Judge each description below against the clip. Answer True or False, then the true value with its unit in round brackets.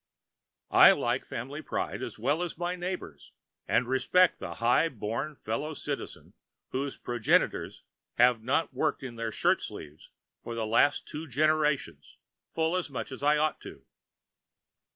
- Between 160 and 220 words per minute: False (150 wpm)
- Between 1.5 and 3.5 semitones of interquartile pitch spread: False (4.5 semitones)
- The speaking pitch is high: False (140 Hz)